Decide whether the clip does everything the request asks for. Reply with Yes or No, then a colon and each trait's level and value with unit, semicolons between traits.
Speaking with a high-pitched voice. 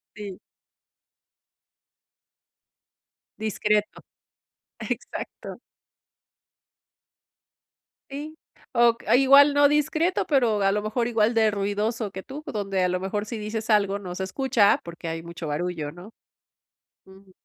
Yes: high, 210 Hz